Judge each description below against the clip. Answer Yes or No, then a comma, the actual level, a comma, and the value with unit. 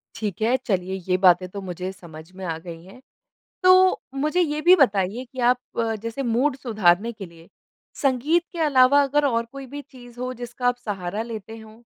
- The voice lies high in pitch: Yes, high, 235 Hz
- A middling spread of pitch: No, wide, 6.3 semitones